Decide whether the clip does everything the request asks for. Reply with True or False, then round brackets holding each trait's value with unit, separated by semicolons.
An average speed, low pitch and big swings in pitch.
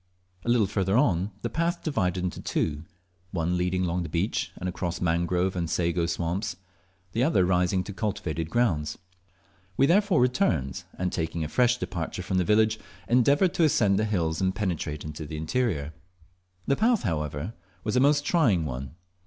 True (170 wpm; 90 Hz; 6.0 semitones)